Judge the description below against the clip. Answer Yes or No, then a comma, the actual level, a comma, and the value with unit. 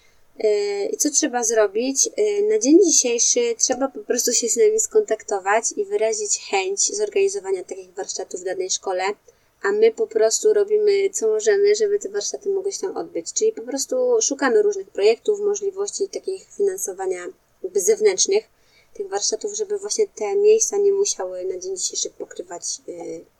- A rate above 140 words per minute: Yes, average, 155 wpm